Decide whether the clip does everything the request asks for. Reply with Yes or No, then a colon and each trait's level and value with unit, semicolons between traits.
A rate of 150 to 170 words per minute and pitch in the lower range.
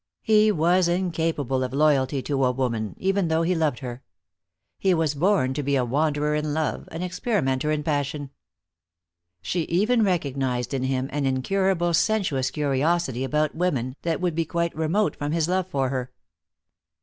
No: average, 165 wpm; medium, 150 Hz